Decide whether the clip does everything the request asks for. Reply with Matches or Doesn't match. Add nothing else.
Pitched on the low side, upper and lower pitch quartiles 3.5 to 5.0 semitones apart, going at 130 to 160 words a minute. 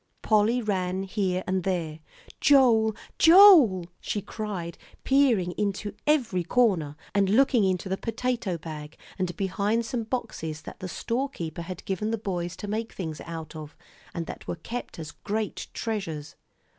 Doesn't match